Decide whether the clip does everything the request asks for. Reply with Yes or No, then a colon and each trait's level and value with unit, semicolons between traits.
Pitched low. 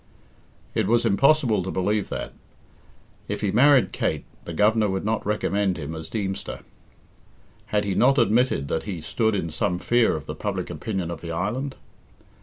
Yes: low, 105 Hz